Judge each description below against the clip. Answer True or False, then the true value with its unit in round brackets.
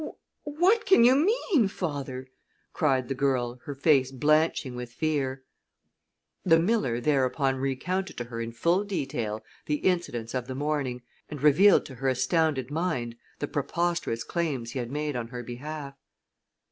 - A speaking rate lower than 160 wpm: True (150 wpm)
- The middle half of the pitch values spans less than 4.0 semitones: False (4.7 semitones)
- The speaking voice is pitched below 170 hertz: True (140 Hz)